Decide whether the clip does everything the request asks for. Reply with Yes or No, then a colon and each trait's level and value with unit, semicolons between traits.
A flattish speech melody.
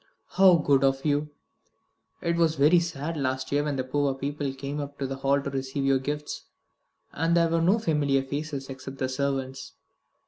Yes: narrow, 2.2 semitones